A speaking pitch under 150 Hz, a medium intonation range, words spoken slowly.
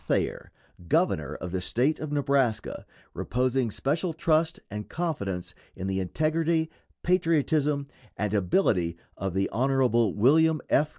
No: low, 135 Hz; wide, 7.7 semitones; slow, 125 wpm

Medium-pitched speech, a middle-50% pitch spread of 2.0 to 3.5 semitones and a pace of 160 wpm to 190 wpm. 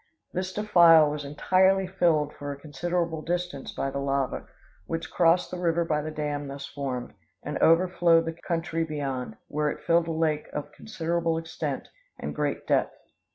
Yes: medium, 160 Hz; average, 2.8 semitones; average, 165 wpm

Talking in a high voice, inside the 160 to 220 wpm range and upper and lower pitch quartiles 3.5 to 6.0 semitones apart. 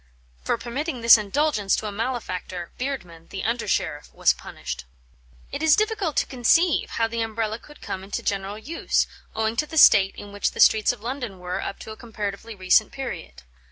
Yes: high, 220 Hz; average, 190 wpm; average, 4.7 semitones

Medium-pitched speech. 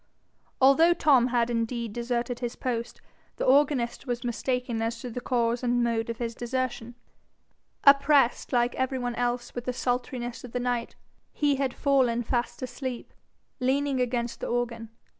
No: high, 245 Hz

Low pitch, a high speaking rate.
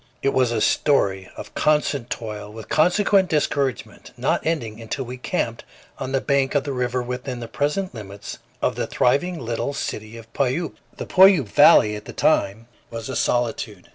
No: low, 125 Hz; average, 175 wpm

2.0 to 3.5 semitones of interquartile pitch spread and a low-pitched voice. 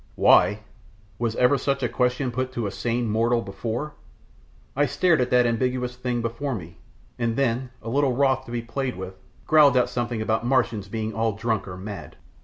Yes: narrow, 2.5 semitones; low, 120 Hz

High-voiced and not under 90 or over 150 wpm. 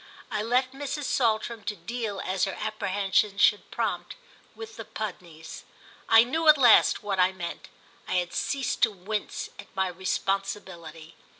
Yes: high, 205 Hz; average, 145 wpm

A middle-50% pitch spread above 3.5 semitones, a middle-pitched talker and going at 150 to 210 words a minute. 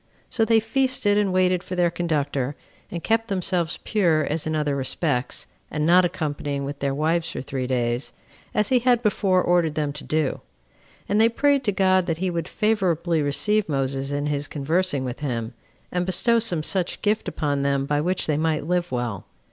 Yes: average, 4.7 semitones; medium, 165 Hz; average, 190 wpm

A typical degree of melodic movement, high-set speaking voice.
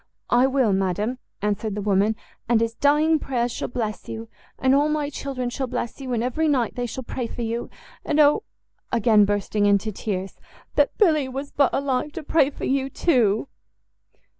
Yes: average, 4.2 semitones; high, 245 Hz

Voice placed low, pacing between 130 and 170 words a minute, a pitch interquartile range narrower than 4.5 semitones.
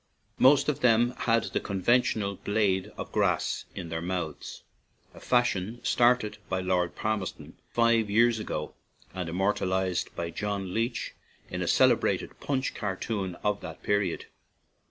Yes: low, 100 Hz; average, 140 wpm; average, 4.0 semitones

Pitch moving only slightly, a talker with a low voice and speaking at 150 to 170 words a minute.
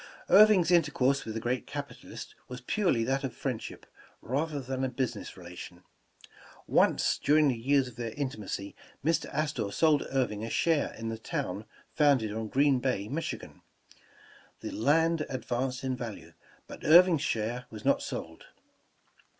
No: average, 4.6 semitones; low, 130 Hz; average, 160 wpm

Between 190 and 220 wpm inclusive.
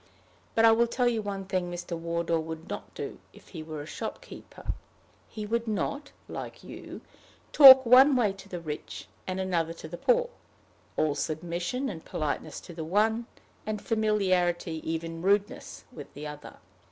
No: average, 175 wpm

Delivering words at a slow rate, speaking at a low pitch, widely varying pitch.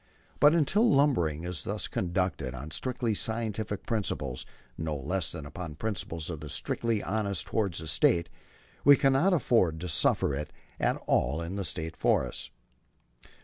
No: average, 150 wpm; very low, 90 Hz; wide, 6.3 semitones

